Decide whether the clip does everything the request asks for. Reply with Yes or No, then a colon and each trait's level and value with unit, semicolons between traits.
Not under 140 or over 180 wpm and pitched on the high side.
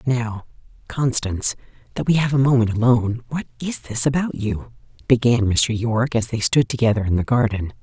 No: average, 175 wpm; low, 120 Hz